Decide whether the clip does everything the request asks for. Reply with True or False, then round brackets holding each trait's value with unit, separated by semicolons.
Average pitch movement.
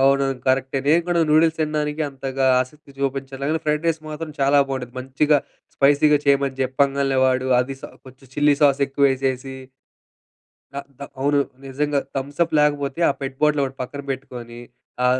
False (1.9 semitones)